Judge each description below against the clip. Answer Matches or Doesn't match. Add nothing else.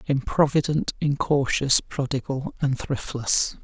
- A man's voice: Matches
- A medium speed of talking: Doesn't match